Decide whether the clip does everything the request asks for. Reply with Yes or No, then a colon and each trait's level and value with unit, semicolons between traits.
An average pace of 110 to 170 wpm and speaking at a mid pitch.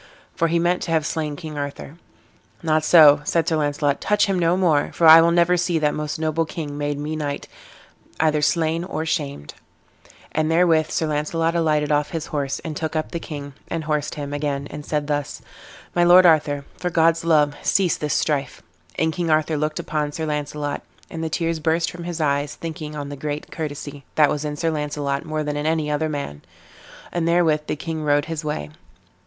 No: fast, 205 wpm; medium, 155 Hz